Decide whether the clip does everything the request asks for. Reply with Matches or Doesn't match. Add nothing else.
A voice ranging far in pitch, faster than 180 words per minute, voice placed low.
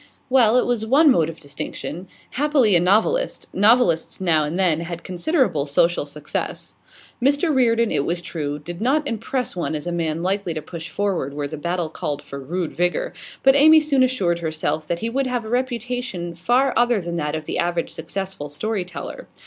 Doesn't match